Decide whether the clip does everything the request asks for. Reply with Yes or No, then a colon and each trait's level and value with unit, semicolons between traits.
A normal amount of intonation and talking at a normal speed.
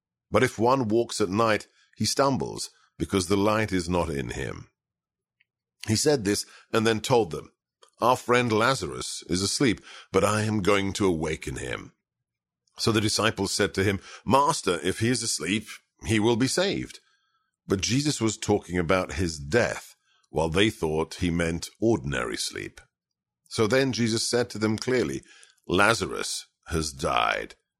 Yes: average, 4.1 semitones; average, 160 wpm